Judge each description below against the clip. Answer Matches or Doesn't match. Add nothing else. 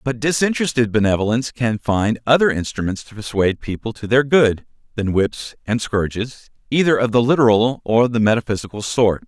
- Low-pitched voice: Matches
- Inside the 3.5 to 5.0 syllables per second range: Doesn't match